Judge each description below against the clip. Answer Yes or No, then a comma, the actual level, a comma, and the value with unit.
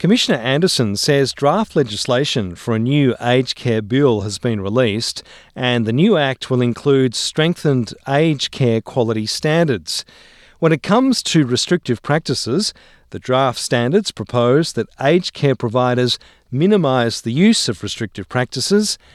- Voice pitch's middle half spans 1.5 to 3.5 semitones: No, average, 5.0 semitones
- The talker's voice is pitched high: No, low, 130 Hz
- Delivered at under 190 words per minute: Yes, average, 140 wpm